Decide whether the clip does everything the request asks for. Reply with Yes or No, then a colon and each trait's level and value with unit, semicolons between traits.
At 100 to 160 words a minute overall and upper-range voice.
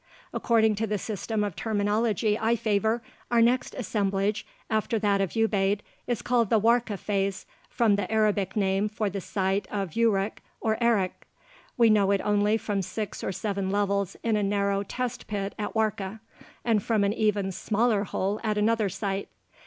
No: average, 170 wpm; high, 210 Hz